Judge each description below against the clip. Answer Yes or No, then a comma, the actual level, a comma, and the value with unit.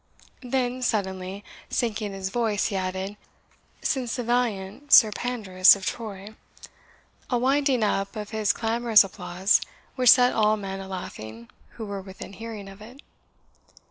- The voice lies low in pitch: No, high, 210 Hz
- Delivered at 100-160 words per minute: Yes, average, 140 wpm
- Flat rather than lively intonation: No, average, 3.9 semitones